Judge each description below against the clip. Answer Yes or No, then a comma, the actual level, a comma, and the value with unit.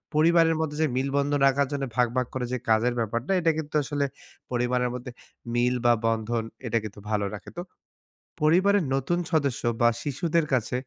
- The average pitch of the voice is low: Yes, low, 130 Hz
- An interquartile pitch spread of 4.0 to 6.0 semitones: Yes, average, 4.3 semitones